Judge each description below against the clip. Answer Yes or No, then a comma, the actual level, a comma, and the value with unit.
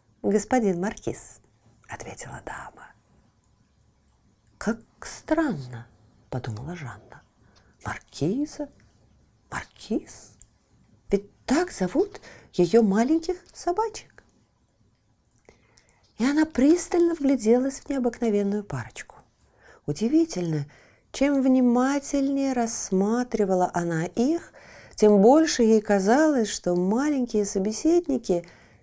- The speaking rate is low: Yes, slow, 75 wpm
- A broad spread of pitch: Yes, wide, 7.7 semitones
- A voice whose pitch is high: Yes, high, 230 Hz